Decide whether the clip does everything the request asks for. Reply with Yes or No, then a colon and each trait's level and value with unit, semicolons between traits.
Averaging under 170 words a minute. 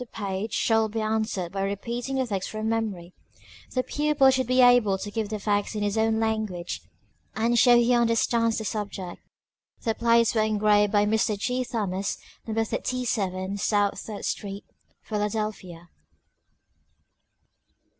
Yes: average, 145 wpm